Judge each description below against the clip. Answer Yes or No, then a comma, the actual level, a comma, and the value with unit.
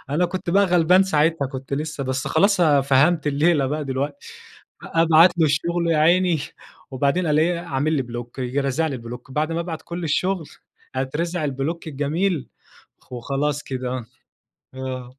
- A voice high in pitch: No, medium, 150 Hz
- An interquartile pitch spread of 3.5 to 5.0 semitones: Yes, average, 4.1 semitones